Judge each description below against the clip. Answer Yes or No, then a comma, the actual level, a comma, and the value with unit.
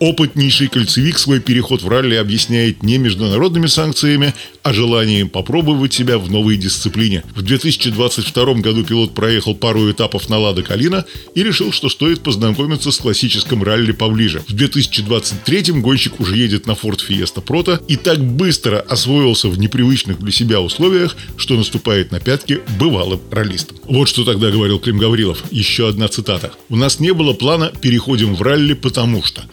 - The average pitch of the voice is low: Yes, low, 120 Hz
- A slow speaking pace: No, fast, 160 wpm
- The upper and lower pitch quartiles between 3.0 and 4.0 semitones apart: No, average, 4.5 semitones